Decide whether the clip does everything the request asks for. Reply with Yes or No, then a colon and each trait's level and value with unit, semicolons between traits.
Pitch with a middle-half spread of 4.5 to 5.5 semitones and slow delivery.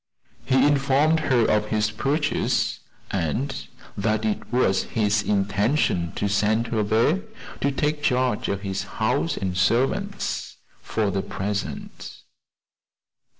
Yes: average, 4.9 semitones; slow, 120 wpm